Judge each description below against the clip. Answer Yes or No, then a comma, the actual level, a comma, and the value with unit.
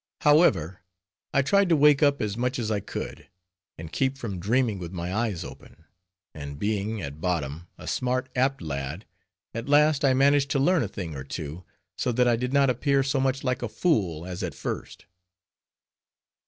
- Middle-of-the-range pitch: No, low, 115 Hz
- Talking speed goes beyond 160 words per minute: Yes, average, 185 wpm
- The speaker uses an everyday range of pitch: No, wide, 7.6 semitones